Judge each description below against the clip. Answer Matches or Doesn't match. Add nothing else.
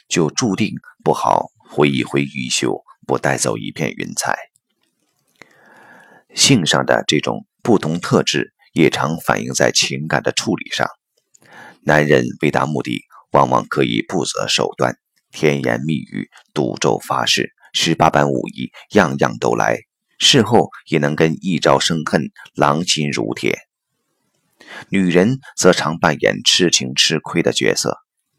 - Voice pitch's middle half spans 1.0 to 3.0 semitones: Matches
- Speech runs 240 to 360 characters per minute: Doesn't match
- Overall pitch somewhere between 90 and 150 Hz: Doesn't match